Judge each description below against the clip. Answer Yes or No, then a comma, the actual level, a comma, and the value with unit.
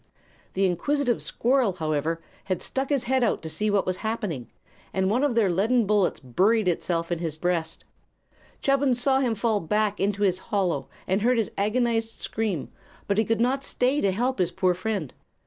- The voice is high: Yes, high, 210 Hz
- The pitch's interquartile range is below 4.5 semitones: No, average, 4.8 semitones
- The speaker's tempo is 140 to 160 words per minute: No, average, 185 wpm